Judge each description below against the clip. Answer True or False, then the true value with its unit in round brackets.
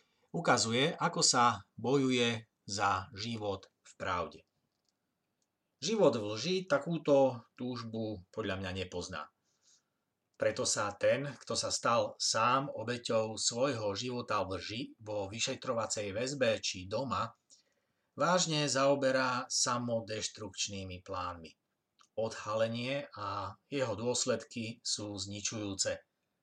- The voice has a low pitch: True (115 Hz)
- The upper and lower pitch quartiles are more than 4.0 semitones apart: True (4.4 semitones)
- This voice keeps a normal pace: False (100 wpm)